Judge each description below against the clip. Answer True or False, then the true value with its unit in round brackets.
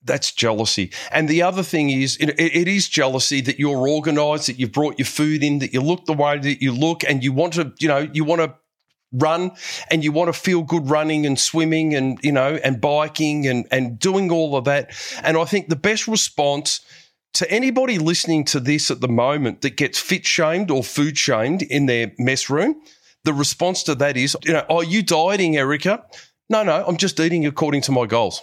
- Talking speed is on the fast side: True (215 wpm)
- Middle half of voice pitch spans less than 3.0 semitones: False (3.4 semitones)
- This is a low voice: False (150 Hz)